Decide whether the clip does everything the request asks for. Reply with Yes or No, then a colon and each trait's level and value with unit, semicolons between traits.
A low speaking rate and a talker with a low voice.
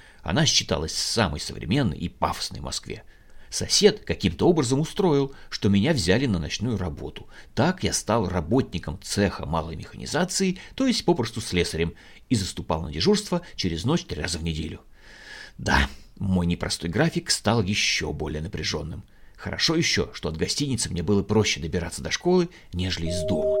No: average, 155 wpm; low, 100 Hz